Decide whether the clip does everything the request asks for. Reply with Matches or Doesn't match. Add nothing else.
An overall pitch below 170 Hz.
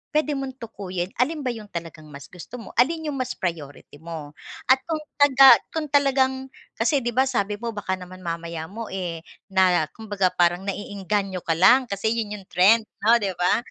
Doesn't match